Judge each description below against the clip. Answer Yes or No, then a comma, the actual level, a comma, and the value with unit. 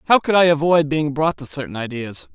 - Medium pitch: Yes, medium, 145 Hz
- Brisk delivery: Yes, fast, 230 wpm